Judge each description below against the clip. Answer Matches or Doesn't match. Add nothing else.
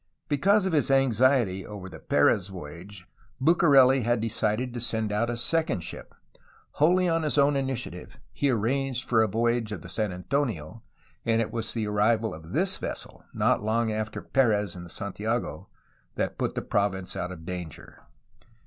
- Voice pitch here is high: Doesn't match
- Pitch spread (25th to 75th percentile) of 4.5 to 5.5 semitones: Matches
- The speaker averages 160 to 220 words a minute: Matches